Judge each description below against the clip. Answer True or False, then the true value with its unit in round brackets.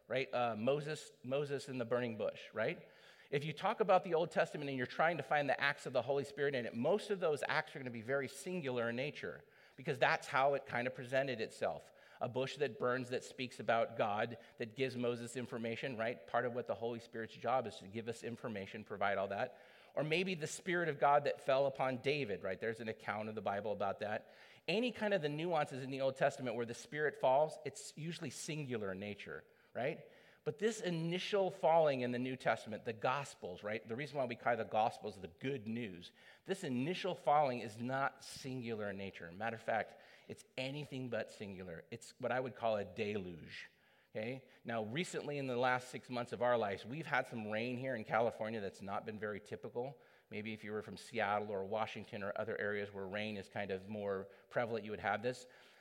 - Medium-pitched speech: False (125 Hz)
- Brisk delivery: True (220 wpm)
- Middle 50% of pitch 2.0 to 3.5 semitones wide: False (4.0 semitones)